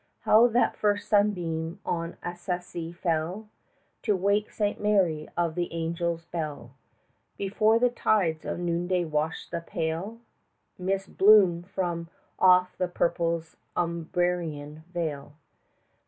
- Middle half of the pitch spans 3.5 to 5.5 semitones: No, average, 2.9 semitones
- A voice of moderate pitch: Yes, medium, 175 Hz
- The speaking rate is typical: No, slow, 120 wpm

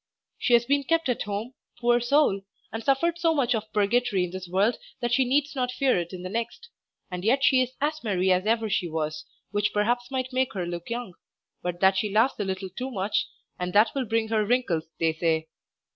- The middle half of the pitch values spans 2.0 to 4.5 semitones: No, average, 5.2 semitones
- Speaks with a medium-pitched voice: No, high, 225 Hz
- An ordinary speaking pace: No, fast, 220 wpm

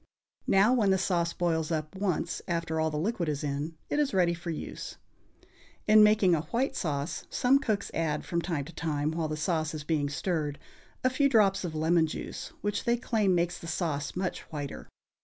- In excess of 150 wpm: Yes, average, 195 wpm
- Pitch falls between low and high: Yes, medium, 170 Hz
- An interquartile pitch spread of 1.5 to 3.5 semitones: No, average, 4.1 semitones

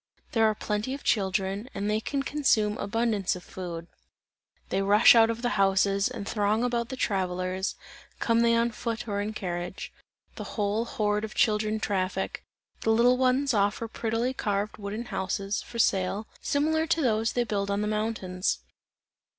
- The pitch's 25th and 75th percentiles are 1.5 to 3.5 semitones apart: Yes, average, 2.8 semitones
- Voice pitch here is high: Yes, high, 215 Hz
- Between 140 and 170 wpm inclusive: Yes, average, 165 wpm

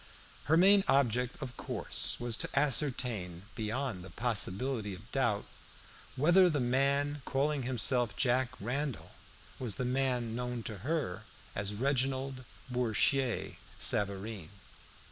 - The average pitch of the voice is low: Yes, low, 125 Hz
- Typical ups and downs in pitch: Yes, average, 3.9 semitones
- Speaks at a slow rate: Yes, slow, 120 wpm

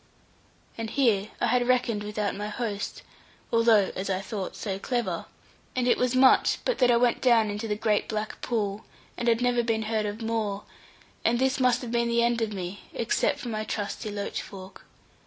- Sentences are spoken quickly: No, average, 195 wpm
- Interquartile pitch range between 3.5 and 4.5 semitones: No, narrow, 2.5 semitones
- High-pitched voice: Yes, high, 225 Hz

